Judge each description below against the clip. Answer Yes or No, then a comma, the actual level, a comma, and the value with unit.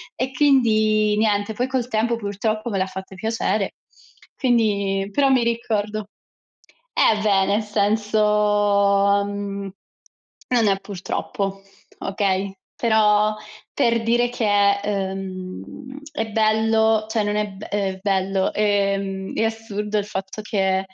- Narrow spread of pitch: Yes, narrow, 1.9 semitones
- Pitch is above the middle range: Yes, high, 210 Hz